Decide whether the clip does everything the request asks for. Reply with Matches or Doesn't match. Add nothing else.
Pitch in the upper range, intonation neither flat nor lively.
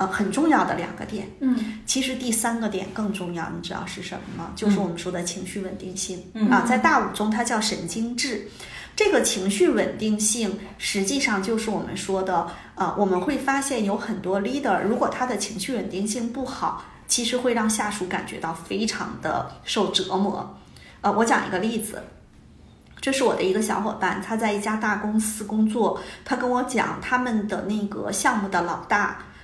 Matches